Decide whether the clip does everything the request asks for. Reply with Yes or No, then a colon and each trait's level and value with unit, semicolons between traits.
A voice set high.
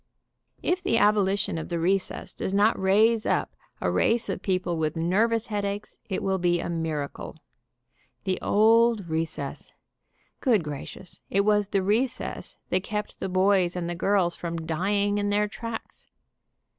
Yes: high, 195 Hz